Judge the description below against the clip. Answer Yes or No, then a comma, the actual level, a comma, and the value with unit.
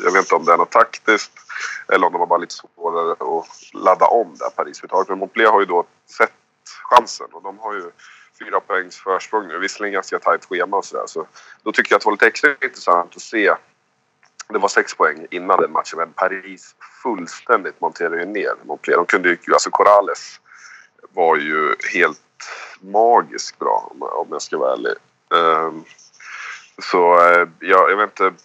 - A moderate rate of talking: Yes, average, 185 wpm